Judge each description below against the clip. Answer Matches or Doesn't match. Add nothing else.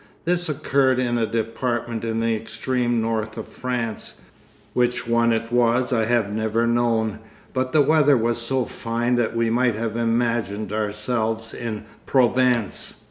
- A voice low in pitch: Matches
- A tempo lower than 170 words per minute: Matches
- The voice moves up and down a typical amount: Doesn't match